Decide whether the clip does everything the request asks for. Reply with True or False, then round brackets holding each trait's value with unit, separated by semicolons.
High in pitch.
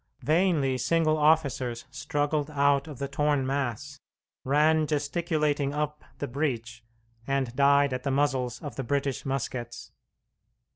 False (140 Hz)